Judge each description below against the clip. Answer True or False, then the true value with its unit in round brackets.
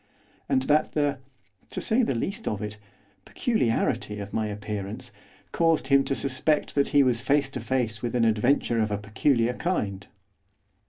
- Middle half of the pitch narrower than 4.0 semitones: False (5.2 semitones)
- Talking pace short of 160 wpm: False (165 wpm)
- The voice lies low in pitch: True (125 Hz)